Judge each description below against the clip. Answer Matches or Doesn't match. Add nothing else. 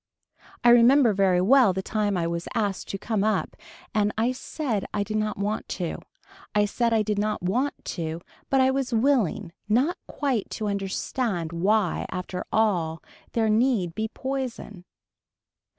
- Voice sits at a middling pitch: Doesn't match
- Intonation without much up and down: Doesn't match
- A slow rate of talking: Doesn't match